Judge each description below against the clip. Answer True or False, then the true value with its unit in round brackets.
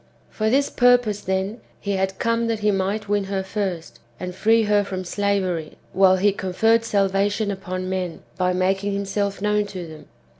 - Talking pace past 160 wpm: True (175 wpm)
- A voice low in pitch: False (200 Hz)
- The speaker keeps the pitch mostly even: True (1.9 semitones)